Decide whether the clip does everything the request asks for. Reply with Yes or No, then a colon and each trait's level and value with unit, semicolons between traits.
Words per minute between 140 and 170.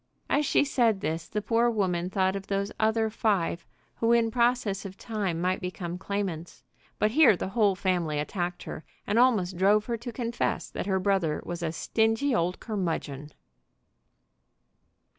Yes: average, 160 wpm